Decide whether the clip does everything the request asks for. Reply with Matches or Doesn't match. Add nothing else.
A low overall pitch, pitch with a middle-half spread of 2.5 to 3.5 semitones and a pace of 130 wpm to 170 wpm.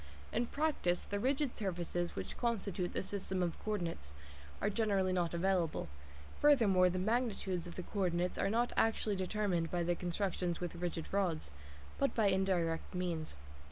Doesn't match